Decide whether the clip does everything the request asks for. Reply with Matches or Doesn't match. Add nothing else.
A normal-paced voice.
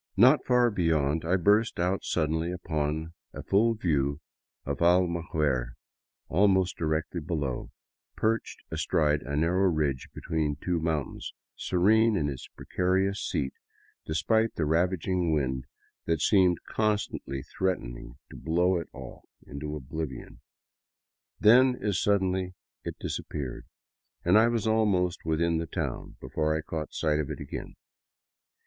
Doesn't match